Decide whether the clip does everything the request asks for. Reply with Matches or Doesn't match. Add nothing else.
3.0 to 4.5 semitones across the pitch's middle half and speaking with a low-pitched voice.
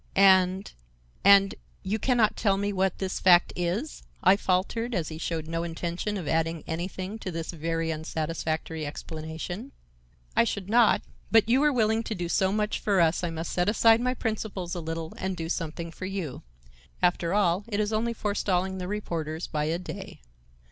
Doesn't match